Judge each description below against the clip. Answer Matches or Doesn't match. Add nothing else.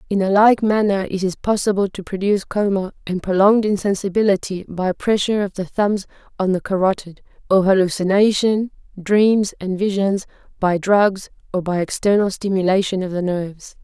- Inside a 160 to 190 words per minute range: Doesn't match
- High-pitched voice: Matches